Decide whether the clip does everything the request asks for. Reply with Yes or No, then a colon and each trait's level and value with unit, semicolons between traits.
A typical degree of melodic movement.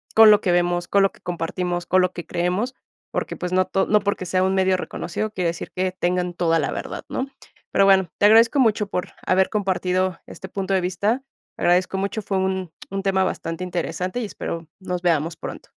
No: narrow, 1.8 semitones